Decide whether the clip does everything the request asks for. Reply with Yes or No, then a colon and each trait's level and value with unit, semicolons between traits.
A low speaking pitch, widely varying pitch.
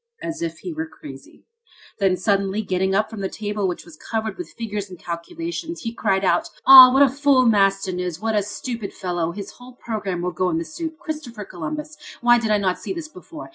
No: high, 215 Hz; wide, 6.2 semitones